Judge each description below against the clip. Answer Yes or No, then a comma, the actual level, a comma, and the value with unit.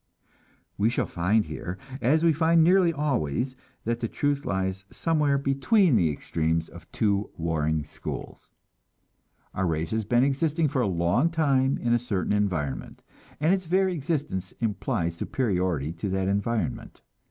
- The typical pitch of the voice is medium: No, low, 115 Hz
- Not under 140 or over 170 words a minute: Yes, average, 150 wpm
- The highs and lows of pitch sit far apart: Yes, wide, 7.9 semitones